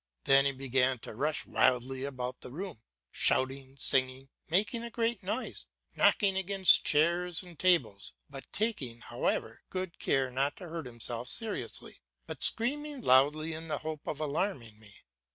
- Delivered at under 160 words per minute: Yes, average, 150 wpm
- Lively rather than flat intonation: Yes, wide, 6.2 semitones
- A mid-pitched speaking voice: Yes, medium, 150 Hz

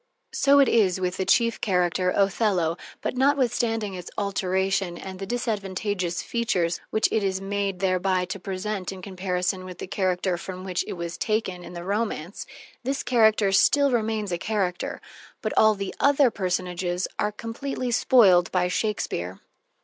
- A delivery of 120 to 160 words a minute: Yes, average, 155 wpm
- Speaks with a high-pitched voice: Yes, high, 195 Hz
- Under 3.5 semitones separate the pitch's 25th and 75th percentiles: Yes, average, 3.1 semitones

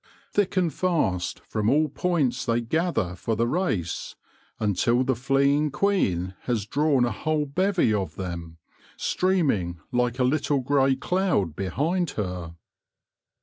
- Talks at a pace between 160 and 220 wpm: No, average, 140 wpm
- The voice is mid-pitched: No, low, 130 Hz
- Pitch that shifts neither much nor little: No, wide, 7.5 semitones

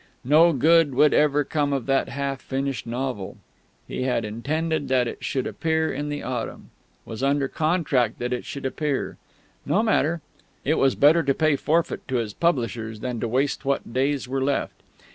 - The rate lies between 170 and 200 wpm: Yes, average, 180 wpm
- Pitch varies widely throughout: No, average, 3.1 semitones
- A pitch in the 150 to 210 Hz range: No, medium, 140 Hz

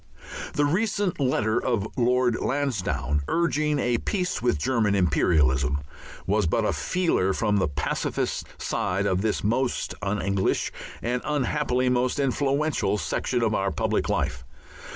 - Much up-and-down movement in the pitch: Yes, wide, 6.6 semitones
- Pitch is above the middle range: No, low, 120 Hz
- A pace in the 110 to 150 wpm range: Yes, slow, 135 wpm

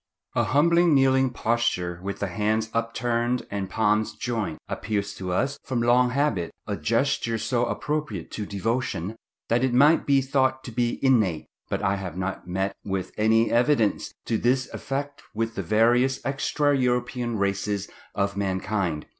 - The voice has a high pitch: No, low, 115 Hz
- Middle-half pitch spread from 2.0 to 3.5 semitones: No, average, 4.6 semitones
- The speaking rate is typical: Yes, average, 155 wpm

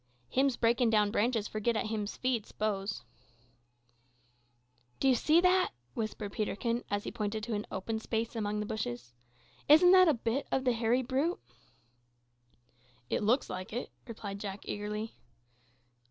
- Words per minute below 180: Yes, average, 155 wpm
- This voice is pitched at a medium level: No, high, 225 Hz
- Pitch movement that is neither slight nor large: Yes, average, 3.2 semitones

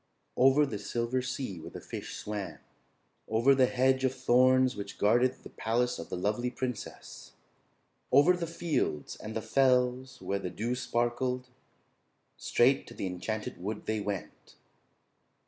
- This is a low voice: Yes, low, 125 Hz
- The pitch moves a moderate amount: Yes, average, 3.4 semitones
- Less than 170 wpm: Yes, average, 145 wpm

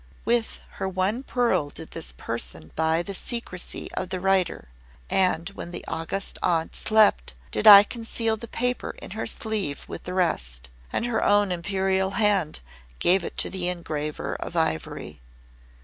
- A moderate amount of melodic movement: Yes, average, 4.3 semitones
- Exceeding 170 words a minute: No, average, 160 wpm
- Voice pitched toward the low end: No, high, 190 Hz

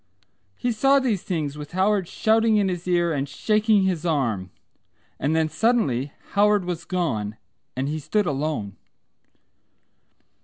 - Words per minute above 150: No, average, 140 wpm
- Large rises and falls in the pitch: Yes, wide, 6.4 semitones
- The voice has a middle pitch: Yes, medium, 175 Hz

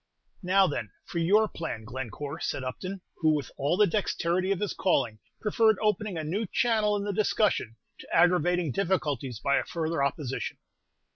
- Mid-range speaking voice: Yes, medium, 175 Hz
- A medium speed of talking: Yes, average, 165 wpm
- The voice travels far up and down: Yes, wide, 6.1 semitones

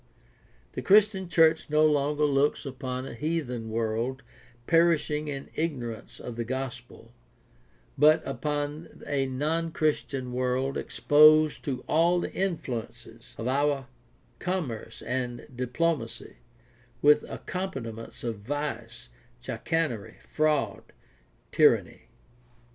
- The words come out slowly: Yes, slow, 105 wpm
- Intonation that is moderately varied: Yes, average, 3.9 semitones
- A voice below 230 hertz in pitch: Yes, medium, 140 Hz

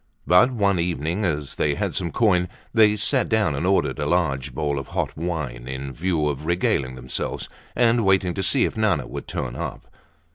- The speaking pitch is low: Yes, very low, 85 Hz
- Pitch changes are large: Yes, wide, 5.9 semitones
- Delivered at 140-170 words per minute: No, average, 190 wpm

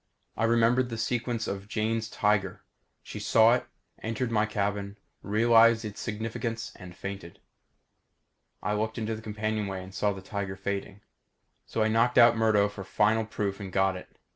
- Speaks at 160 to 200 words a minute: Yes, average, 165 wpm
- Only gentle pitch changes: Yes, narrow, 2.2 semitones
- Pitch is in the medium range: No, low, 110 Hz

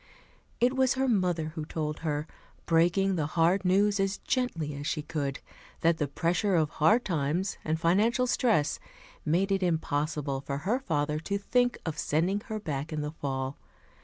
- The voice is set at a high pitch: No, medium, 165 Hz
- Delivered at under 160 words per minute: No, average, 170 wpm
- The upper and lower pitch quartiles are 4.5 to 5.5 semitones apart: Yes, average, 4.9 semitones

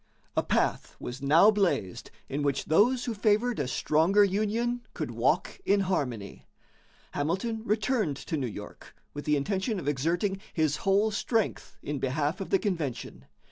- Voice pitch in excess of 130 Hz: Yes, medium, 185 Hz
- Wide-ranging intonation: Yes, wide, 6.6 semitones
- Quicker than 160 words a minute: No, average, 155 wpm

